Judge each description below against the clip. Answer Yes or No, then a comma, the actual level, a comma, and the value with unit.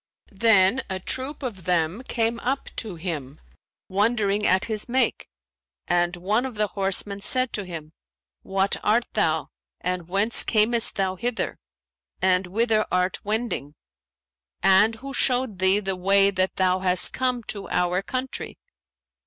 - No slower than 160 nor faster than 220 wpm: No, average, 145 wpm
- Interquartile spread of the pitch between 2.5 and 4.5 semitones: Yes, average, 3.9 semitones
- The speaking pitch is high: Yes, high, 200 Hz